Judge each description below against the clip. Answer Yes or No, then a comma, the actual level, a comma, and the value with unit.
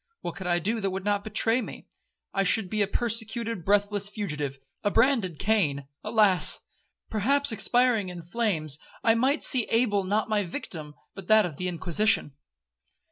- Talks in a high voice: Yes, high, 205 Hz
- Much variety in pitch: No, average, 4.0 semitones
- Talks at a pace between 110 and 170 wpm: Yes, average, 155 wpm